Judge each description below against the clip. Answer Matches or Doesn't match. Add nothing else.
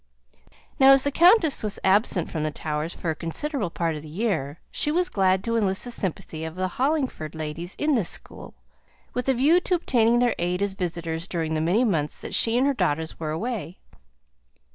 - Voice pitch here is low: Doesn't match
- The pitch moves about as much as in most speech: Doesn't match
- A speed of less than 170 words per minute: Doesn't match